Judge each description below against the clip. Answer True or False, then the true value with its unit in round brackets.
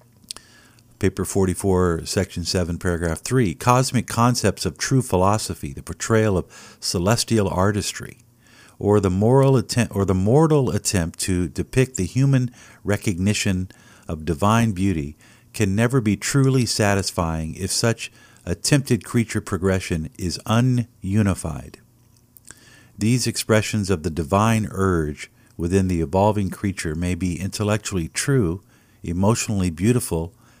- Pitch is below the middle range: True (105 Hz)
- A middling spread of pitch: True (4.3 semitones)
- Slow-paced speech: True (120 wpm)